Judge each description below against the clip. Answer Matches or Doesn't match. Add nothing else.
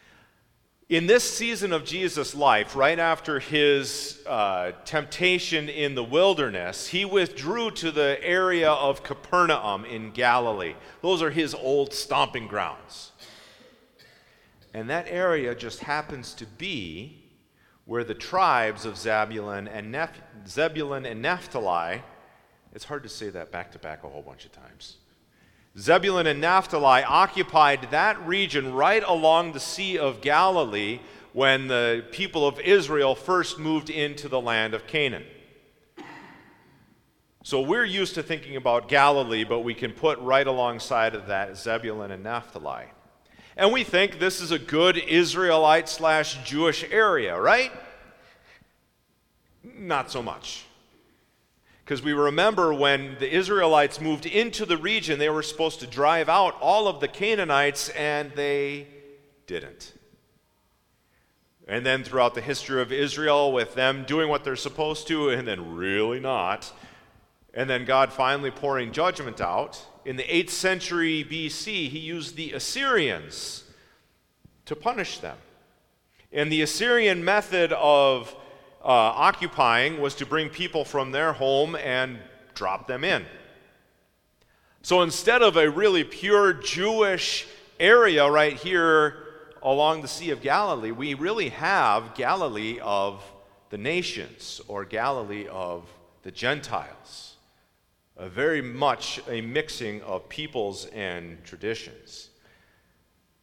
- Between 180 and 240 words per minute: Doesn't match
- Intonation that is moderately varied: Matches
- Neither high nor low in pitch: Matches